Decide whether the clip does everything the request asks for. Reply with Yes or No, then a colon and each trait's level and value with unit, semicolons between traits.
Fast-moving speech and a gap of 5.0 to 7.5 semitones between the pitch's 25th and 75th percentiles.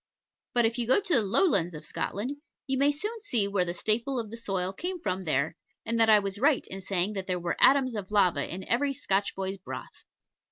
Yes: fast, 230 wpm; wide, 5.6 semitones